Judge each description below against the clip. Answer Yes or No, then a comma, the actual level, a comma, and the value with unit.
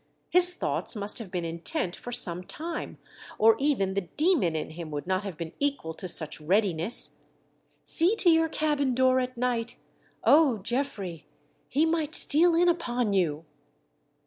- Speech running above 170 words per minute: No, average, 165 wpm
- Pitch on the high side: Yes, high, 240 Hz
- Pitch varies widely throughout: Yes, wide, 9.0 semitones